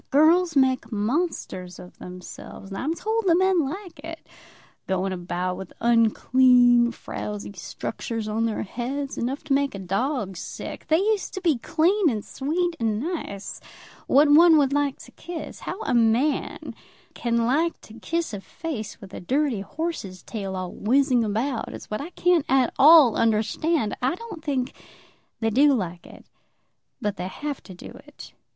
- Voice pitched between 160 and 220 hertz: No, very high, 255 Hz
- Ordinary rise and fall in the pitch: No, wide, 7.0 semitones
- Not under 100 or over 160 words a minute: No, average, 170 wpm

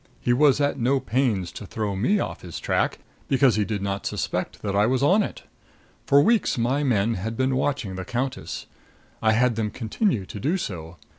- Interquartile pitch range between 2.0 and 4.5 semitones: No, average, 5.0 semitones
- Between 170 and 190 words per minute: No, average, 200 wpm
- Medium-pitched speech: No, low, 120 Hz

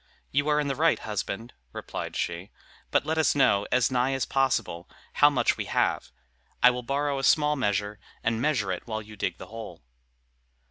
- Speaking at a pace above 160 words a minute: Yes, average, 190 wpm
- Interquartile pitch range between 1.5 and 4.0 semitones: No, average, 5.2 semitones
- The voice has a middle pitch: No, low, 125 Hz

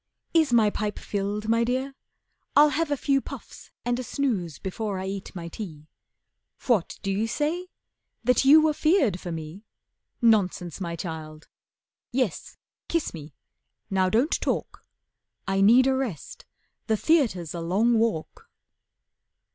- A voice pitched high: Yes, high, 215 Hz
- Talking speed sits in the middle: Yes, average, 145 wpm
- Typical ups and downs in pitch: No, wide, 6.5 semitones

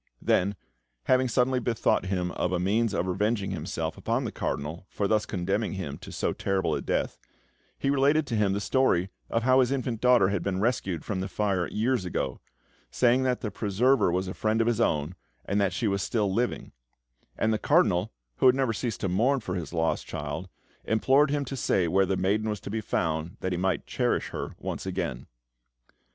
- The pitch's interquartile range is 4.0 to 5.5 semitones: Yes, average, 4.5 semitones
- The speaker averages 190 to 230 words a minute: Yes, fast, 205 wpm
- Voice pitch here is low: Yes, low, 105 Hz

